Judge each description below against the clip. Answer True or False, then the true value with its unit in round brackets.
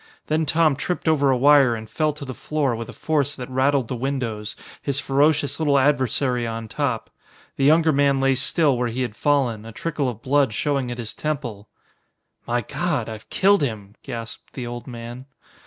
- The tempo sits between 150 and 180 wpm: False (190 wpm)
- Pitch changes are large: False (3.5 semitones)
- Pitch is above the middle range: False (135 Hz)